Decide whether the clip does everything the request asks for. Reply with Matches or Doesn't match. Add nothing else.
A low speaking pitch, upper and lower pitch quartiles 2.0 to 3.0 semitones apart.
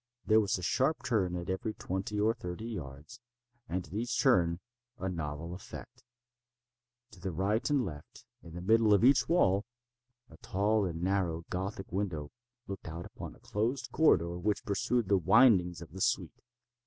Doesn't match